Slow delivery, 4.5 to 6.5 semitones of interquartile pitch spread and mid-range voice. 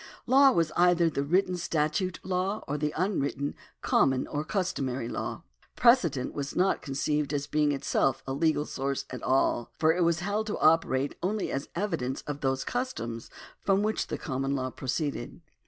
No: average, 170 wpm; average, 5.1 semitones; medium, 150 Hz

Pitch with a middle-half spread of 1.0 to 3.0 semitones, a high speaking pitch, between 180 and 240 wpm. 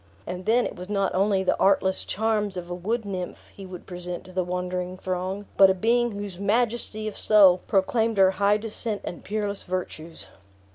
Yes: average, 2.7 semitones; high, 195 Hz; average, 190 wpm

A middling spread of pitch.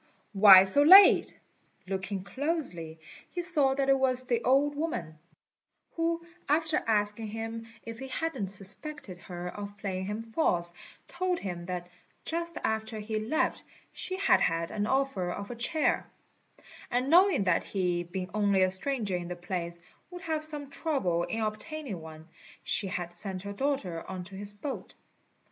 No: wide, 7.4 semitones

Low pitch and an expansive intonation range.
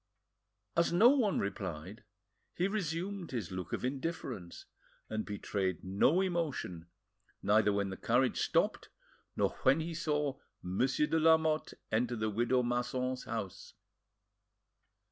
Yes: low, 125 Hz; wide, 8.1 semitones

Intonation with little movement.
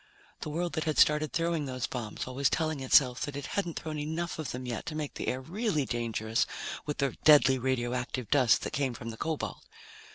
No: average, 3.8 semitones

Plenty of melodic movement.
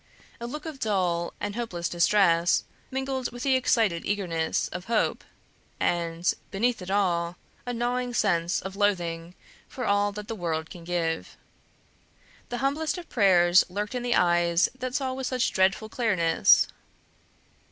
Yes: wide, 5.9 semitones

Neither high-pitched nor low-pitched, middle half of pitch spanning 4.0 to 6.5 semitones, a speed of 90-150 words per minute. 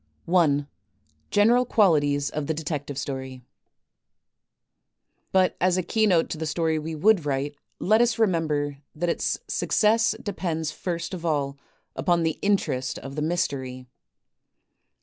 Yes: medium, 160 Hz; average, 4.3 semitones; slow, 135 wpm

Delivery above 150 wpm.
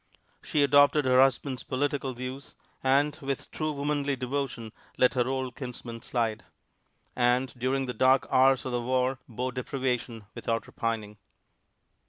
No: average, 140 wpm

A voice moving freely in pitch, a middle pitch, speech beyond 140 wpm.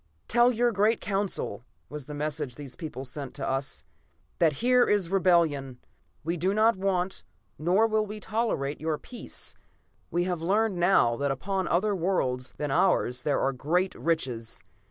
Yes: wide, 6.1 semitones; medium, 170 Hz; average, 160 wpm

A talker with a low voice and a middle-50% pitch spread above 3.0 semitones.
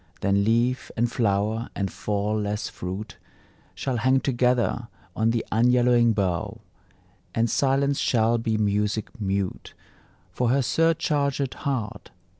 Yes: low, 115 Hz; average, 3.4 semitones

